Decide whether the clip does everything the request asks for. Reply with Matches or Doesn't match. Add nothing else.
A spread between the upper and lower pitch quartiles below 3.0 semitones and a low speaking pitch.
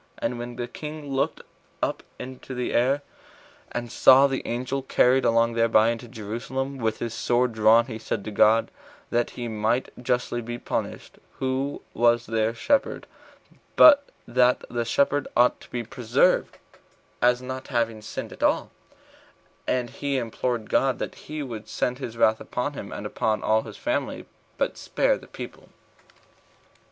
Matches